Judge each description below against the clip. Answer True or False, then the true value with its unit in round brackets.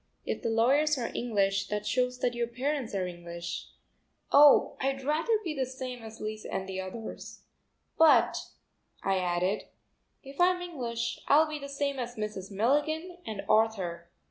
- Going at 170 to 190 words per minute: False (160 wpm)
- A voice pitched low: False (240 Hz)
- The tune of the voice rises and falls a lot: True (5.8 semitones)